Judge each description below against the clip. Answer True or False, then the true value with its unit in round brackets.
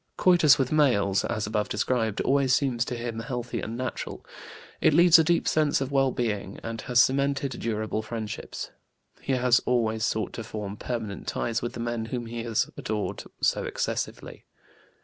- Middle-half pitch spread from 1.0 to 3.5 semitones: True (3.2 semitones)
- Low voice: True (120 Hz)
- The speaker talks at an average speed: True (170 wpm)